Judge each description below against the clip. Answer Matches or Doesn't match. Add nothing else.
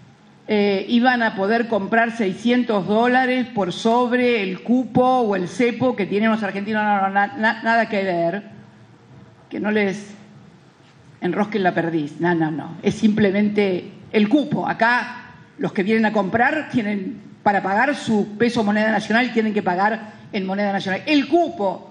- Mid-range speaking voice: Doesn't match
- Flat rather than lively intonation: Doesn't match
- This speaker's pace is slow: Doesn't match